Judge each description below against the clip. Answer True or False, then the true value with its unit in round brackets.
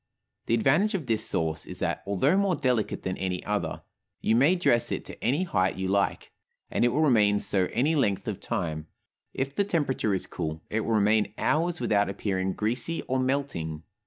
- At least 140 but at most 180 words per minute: False (190 wpm)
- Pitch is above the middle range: False (110 Hz)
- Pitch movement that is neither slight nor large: False (6.7 semitones)